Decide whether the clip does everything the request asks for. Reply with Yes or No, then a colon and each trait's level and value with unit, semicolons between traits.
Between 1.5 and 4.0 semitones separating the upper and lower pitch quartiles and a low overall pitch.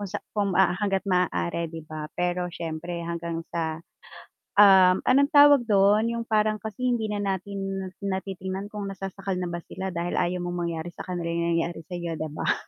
No: average, 2.9 semitones; medium, 185 Hz